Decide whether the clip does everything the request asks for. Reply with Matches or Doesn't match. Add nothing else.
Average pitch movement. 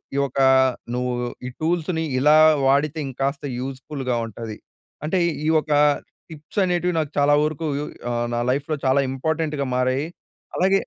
Matches